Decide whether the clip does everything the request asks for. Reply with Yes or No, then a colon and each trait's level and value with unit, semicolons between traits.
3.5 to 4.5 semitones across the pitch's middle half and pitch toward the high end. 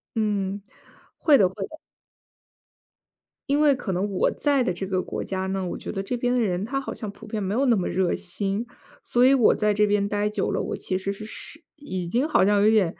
Yes: average, 4.1 semitones; high, 205 Hz